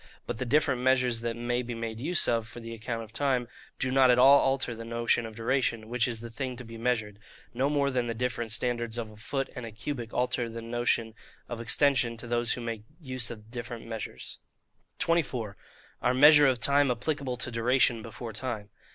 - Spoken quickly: Yes, fast, 210 wpm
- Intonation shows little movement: Yes, narrow, 2.1 semitones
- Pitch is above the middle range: No, low, 120 Hz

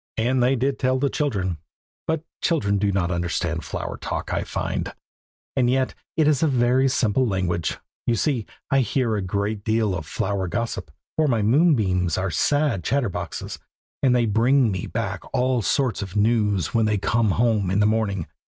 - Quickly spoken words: No, average, 180 wpm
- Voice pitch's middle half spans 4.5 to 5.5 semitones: Yes, average, 4.9 semitones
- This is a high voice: No, low, 110 Hz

